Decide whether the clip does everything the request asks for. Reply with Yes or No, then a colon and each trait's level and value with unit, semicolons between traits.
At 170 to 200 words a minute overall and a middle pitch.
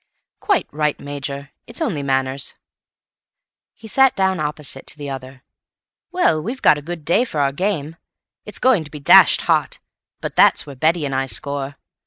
Yes: average, 175 wpm; medium, 150 Hz